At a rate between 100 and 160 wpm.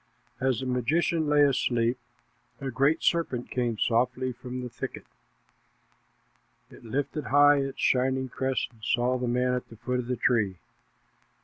Yes: average, 150 wpm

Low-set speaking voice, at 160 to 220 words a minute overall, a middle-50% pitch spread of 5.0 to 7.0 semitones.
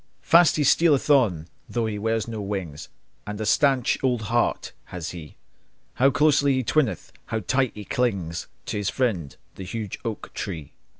Yes: low, 110 Hz; average, 170 wpm; average, 5.3 semitones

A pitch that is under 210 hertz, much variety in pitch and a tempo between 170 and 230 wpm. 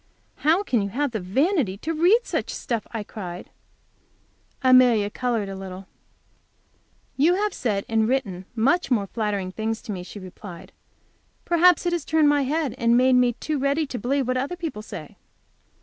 No: high, 245 Hz; wide, 6.2 semitones; average, 175 wpm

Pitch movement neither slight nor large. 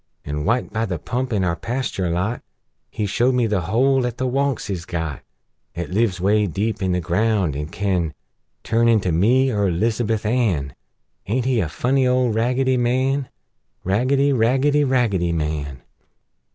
No: wide, 5.9 semitones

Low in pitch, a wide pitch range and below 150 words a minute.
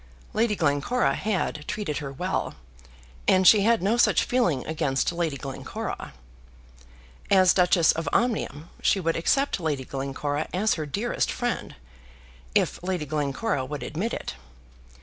No: medium, 170 Hz; wide, 6.2 semitones; slow, 135 wpm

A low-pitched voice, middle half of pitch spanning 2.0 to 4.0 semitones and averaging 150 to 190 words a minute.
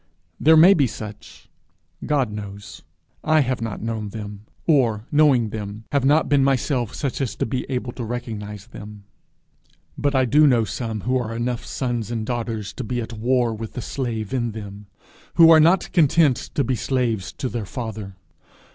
Yes: low, 120 Hz; average, 3.7 semitones; average, 180 wpm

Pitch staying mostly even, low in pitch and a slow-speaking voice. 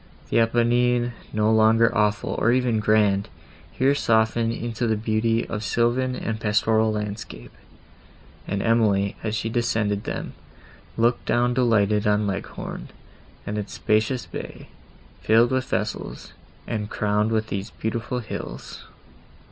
Yes: narrow, 2.0 semitones; low, 110 Hz; slow, 130 wpm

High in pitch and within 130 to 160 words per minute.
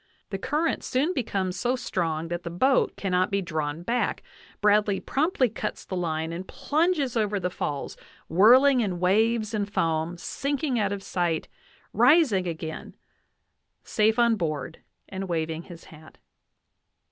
Yes: high, 195 Hz; average, 145 wpm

